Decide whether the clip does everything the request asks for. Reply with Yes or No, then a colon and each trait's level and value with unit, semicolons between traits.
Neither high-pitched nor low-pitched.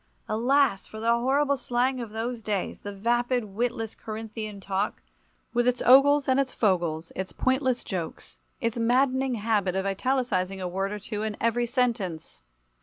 No: high, 230 Hz